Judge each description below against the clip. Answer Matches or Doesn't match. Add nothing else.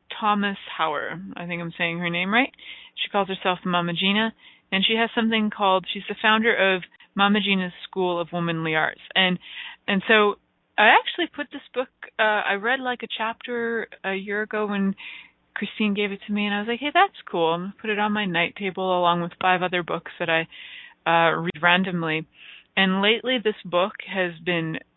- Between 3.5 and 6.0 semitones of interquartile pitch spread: Matches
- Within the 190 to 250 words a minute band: Matches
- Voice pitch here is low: Doesn't match